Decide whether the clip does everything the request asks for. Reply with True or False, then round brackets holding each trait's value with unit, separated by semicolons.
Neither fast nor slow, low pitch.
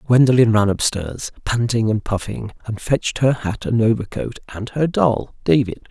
True (165 wpm; 115 Hz)